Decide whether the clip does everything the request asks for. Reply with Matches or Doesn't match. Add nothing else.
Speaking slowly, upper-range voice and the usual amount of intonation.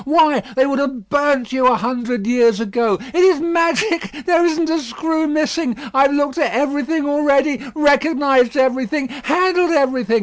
Doesn't match